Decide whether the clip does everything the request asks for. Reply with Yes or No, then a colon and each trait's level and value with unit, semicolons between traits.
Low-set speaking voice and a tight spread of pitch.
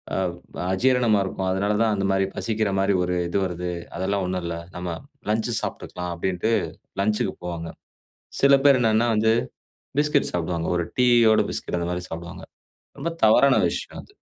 No: very low, 95 Hz; average, 4.0 semitones